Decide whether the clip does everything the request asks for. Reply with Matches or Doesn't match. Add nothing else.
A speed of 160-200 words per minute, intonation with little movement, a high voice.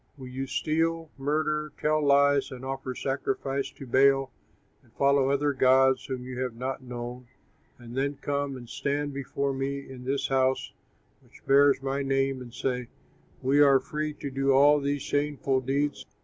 Doesn't match